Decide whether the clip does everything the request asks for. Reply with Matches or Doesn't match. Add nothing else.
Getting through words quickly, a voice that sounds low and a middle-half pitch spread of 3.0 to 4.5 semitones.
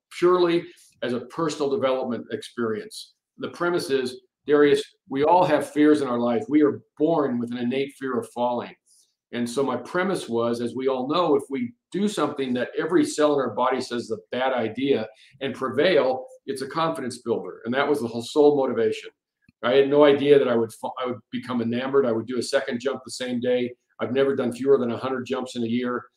Matches